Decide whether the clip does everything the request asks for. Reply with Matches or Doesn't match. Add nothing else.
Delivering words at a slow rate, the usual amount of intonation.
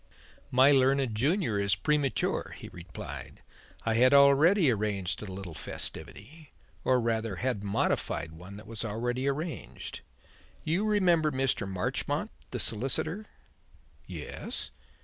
Doesn't match